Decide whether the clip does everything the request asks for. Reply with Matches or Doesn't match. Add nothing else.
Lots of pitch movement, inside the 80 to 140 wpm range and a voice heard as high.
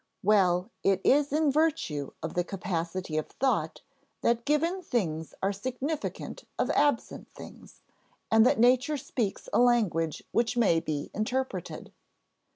Matches